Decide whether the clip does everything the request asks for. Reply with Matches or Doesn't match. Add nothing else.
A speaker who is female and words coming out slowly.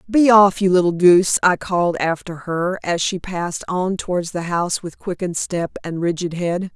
Doesn't match